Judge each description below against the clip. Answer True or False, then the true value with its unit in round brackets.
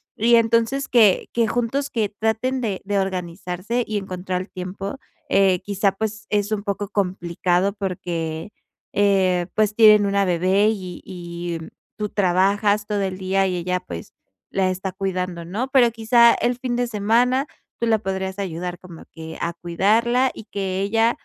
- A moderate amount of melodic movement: True (3.3 semitones)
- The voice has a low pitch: False (200 Hz)